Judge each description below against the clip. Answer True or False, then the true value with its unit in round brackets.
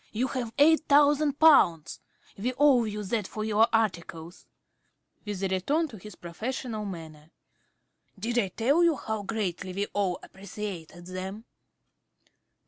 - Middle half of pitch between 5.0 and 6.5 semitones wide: True (5.4 semitones)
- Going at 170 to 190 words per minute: False (135 wpm)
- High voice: True (210 Hz)